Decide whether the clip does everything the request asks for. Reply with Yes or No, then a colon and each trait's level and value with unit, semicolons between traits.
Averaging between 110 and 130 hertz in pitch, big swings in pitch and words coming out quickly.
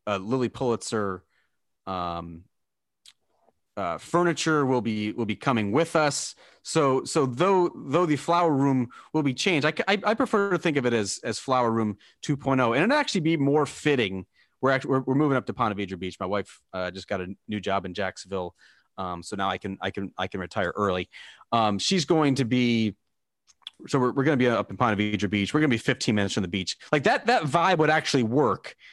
Yes: low, 120 Hz; wide, 7.4 semitones; fast, 220 wpm